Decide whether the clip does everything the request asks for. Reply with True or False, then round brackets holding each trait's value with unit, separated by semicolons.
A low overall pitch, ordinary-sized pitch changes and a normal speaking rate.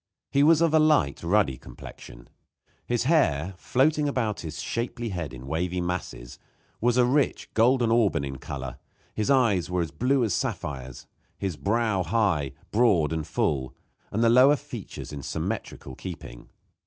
False (100 Hz; 8.4 semitones; 155 wpm)